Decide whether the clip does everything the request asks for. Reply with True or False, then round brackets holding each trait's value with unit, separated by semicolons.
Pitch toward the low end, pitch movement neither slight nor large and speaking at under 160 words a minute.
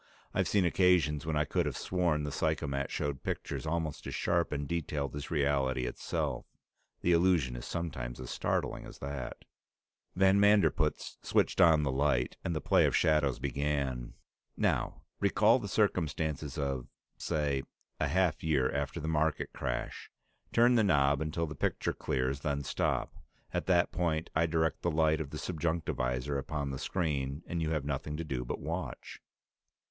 False (75 Hz; 3.4 semitones; 165 wpm)